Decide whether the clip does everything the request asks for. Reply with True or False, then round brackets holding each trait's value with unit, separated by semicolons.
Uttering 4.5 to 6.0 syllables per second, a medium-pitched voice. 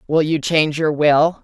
True (4.7 syllables/s; 155 Hz)